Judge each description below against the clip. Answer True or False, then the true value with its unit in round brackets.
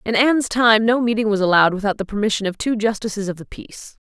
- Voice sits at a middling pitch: False (215 Hz)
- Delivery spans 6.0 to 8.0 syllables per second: True (6.7 syllables/s)